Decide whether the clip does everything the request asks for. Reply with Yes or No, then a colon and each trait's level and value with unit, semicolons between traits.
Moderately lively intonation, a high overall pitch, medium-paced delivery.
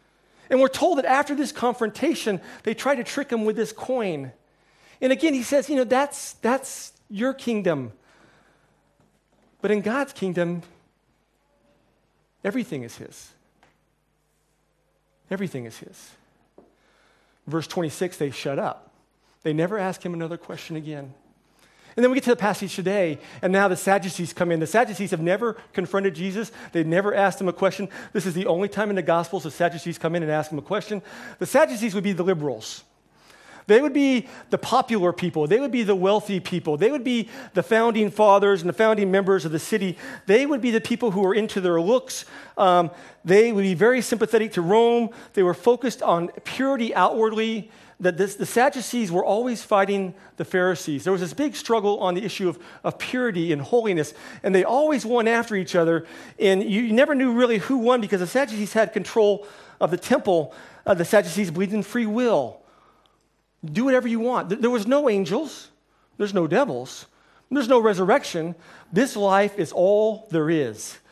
Yes: average, 4.9 semitones; high, 205 Hz; average, 185 wpm